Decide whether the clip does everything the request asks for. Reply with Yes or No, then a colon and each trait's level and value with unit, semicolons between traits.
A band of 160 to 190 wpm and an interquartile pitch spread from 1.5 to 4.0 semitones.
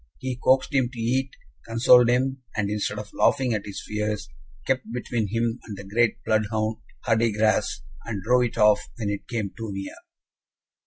Yes: average, 170 wpm; narrow, 2.6 semitones